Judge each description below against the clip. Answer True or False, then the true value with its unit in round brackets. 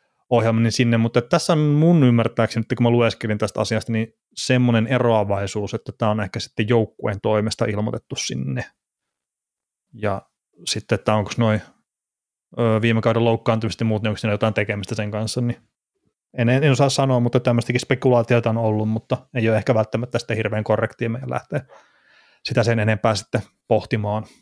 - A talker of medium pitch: False (115 Hz)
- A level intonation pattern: True (1.9 semitones)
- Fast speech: True (160 wpm)